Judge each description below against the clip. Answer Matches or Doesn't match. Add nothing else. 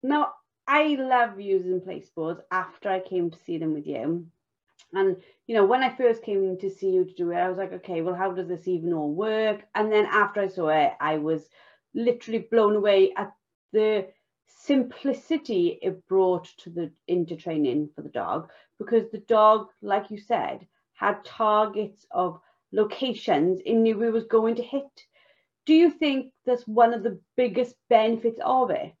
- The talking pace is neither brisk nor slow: Matches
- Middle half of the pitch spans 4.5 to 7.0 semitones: Matches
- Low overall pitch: Doesn't match